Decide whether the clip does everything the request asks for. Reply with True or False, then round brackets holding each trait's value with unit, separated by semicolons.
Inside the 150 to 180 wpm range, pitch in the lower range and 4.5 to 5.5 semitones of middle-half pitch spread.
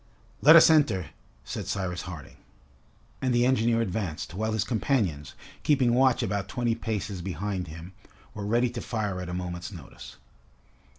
True (155 wpm; 105 Hz; 4.9 semitones)